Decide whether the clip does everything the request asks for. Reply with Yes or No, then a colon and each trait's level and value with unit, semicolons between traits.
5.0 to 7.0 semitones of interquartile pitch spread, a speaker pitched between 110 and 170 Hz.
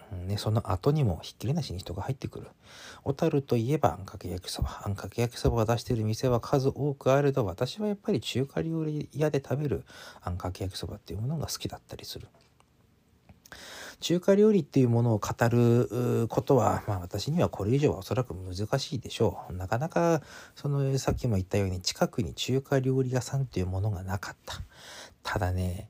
Yes: wide, 5.6 semitones; low, 120 Hz